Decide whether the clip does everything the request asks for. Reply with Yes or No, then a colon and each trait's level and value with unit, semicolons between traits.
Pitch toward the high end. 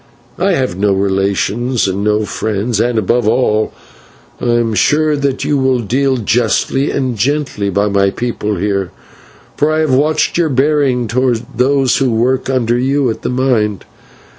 No: low, 120 Hz